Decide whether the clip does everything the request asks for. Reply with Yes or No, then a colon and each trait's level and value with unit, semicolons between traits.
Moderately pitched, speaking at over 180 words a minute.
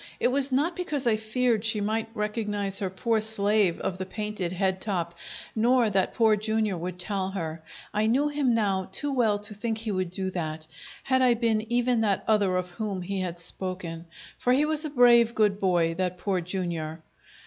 No: high, 210 Hz; average, 195 wpm